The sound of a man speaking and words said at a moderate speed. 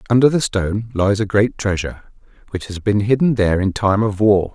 No: male; fast, 210 wpm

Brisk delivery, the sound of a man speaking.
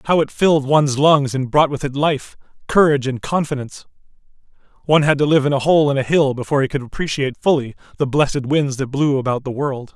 Yes: fast, 215 wpm; male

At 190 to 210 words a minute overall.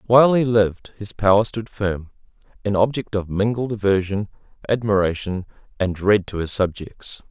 No: average, 150 wpm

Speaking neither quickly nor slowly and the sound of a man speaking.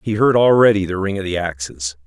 No: fast, 235 wpm; male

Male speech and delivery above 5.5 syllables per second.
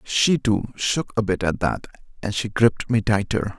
No: male; 4.5 syllables/s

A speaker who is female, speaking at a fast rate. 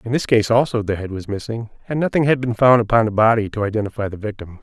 No: male; fast, 260 wpm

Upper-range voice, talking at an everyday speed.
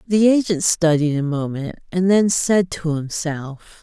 No: medium, 170 Hz; average, 155 wpm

